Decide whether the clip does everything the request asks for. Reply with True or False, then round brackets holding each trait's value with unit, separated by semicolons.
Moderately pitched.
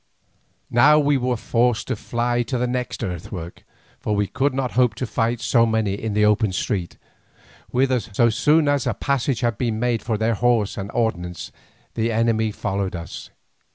False (115 Hz)